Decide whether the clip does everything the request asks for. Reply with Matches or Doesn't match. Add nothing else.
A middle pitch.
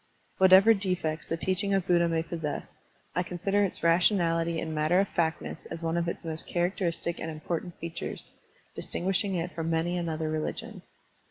Matches